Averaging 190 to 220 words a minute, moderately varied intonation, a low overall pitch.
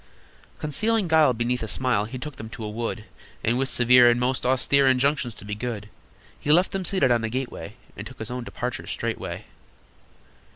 Yes: average, 195 wpm; average, 3.3 semitones; low, 125 Hz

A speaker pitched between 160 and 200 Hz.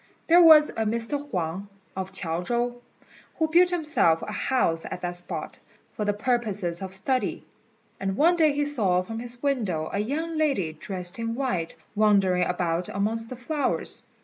No: high, 220 Hz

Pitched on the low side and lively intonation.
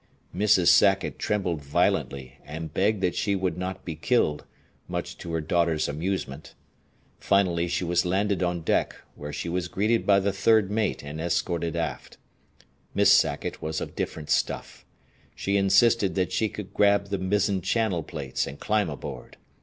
No: very low, 90 Hz; average, 3.5 semitones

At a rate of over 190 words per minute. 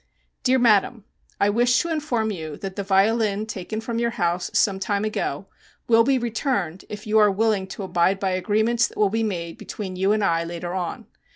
Yes: average, 200 wpm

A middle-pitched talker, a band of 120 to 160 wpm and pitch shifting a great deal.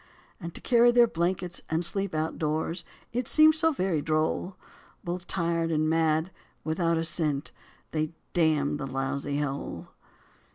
No: medium, 165 Hz; average, 140 wpm; average, 2.9 semitones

